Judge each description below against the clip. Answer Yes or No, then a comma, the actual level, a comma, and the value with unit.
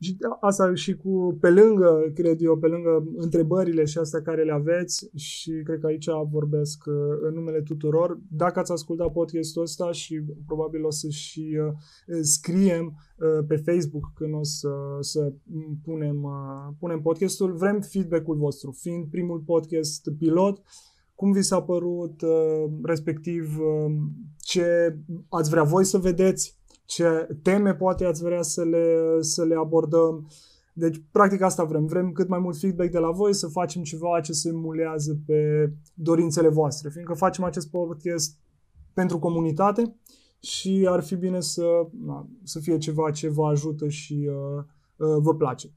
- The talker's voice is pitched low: No, medium, 165 Hz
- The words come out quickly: No, average, 150 wpm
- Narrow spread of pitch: Yes, narrow, 2.3 semitones